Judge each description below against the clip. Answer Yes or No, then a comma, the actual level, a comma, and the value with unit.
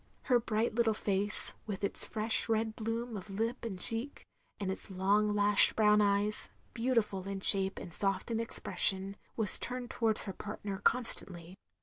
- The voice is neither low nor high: No, high, 210 Hz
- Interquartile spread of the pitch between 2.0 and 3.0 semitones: Yes, narrow, 2.5 semitones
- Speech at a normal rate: Yes, average, 170 wpm